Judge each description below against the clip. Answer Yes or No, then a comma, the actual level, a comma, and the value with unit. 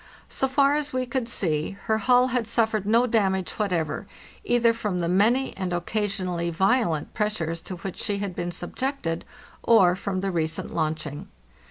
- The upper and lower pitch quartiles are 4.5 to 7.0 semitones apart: Yes, average, 5.1 semitones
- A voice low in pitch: No, high, 200 Hz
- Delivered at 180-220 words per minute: No, average, 165 wpm